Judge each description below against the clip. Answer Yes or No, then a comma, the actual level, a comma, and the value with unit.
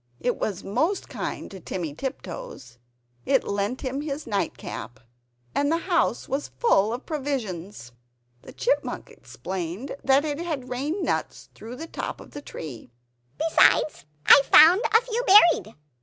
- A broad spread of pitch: Yes, wide, 8.1 semitones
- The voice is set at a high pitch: Yes, very high, 265 Hz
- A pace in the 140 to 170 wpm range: Yes, average, 145 wpm